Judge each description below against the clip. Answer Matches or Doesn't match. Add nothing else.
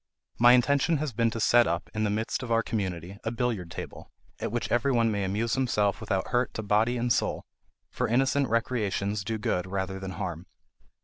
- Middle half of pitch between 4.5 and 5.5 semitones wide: Doesn't match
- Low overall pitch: Matches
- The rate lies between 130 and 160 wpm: Doesn't match